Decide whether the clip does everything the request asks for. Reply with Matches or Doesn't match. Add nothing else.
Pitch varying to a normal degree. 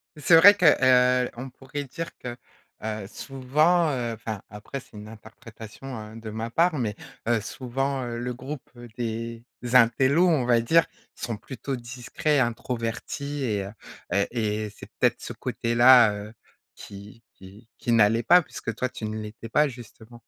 Matches